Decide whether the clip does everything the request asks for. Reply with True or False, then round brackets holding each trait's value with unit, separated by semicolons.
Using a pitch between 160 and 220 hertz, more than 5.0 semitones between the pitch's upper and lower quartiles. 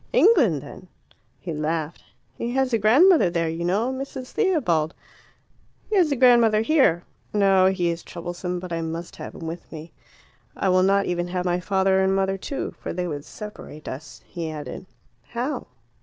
True (185 Hz; 5.5 semitones)